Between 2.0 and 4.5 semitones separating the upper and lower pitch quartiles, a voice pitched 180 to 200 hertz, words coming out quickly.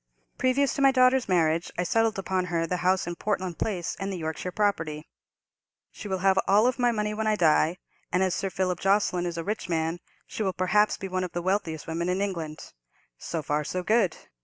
Yes: average, 3.5 semitones; medium, 185 Hz; fast, 210 wpm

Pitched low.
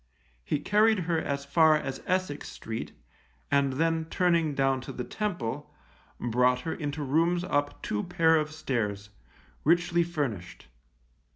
No: medium, 150 Hz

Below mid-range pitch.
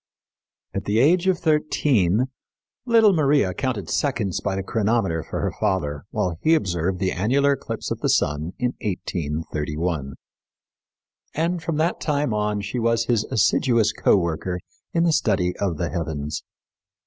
Yes: low, 105 Hz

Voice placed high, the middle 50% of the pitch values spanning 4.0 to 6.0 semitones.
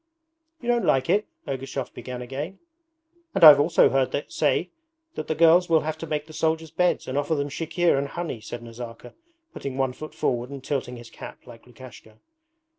No: medium, 140 Hz; average, 4.3 semitones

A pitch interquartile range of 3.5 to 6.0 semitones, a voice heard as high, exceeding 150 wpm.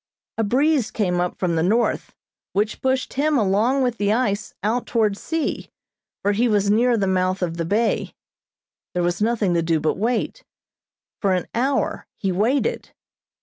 Yes: average, 4.6 semitones; high, 210 Hz; average, 170 wpm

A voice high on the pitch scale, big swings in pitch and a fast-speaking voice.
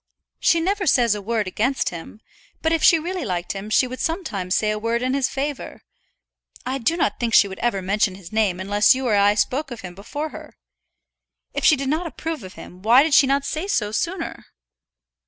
Yes: high, 240 Hz; wide, 6.7 semitones; fast, 215 wpm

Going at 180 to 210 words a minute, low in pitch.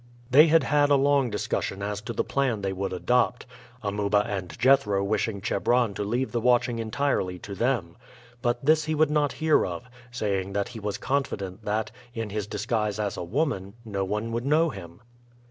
Yes: average, 190 wpm; low, 110 Hz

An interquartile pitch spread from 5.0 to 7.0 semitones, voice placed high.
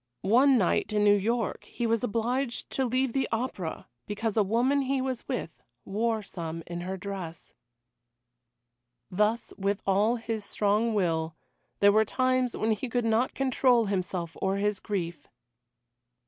No: average, 3.9 semitones; high, 215 Hz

